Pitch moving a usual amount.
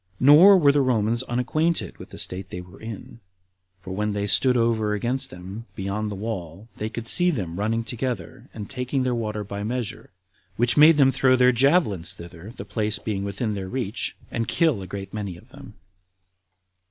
Yes: average, 4.2 semitones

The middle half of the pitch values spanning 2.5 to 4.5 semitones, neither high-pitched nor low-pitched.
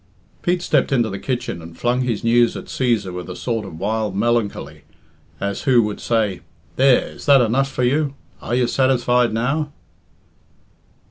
No: average, 3.5 semitones; low, 120 Hz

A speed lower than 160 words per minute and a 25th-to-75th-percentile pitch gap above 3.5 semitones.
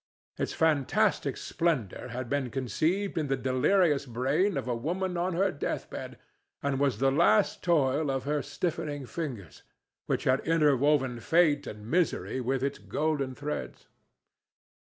Yes: average, 145 wpm; average, 3.9 semitones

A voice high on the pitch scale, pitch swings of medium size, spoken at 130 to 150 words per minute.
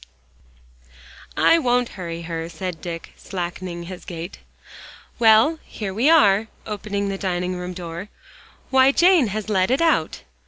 Yes: high, 195 Hz; average, 4.8 semitones; slow, 135 wpm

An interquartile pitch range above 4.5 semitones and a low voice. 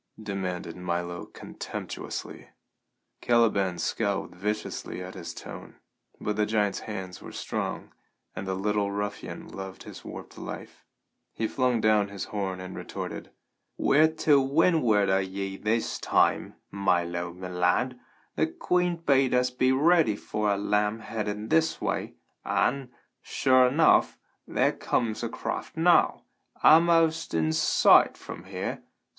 Yes: average, 5.2 semitones; low, 105 Hz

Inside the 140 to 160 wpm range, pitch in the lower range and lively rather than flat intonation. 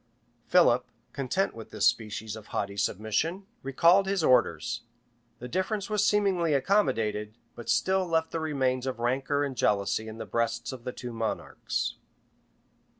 Yes: average, 150 wpm; low, 130 Hz; wide, 6.9 semitones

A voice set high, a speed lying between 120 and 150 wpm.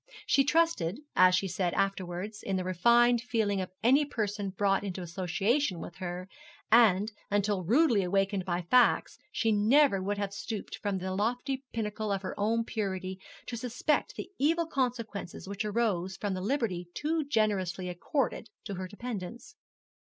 No: high, 205 Hz; average, 160 wpm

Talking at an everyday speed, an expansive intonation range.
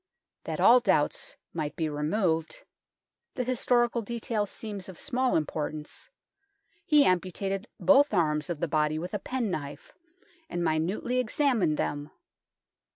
No: slow, 130 wpm; wide, 7.4 semitones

